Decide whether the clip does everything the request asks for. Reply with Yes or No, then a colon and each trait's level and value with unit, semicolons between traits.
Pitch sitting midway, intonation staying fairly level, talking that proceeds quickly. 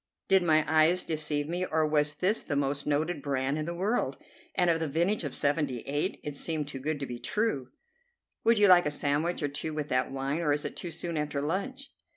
No: medium, 155 Hz; average, 3.1 semitones; fast, 220 wpm